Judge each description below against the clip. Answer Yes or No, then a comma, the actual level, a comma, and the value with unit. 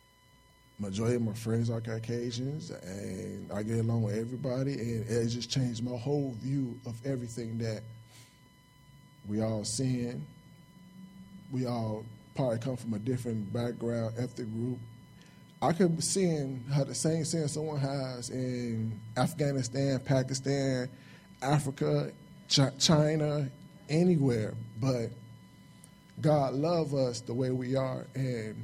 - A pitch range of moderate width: Yes, average, 3.7 semitones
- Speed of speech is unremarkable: No, slow, 130 wpm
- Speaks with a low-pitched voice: Yes, low, 130 Hz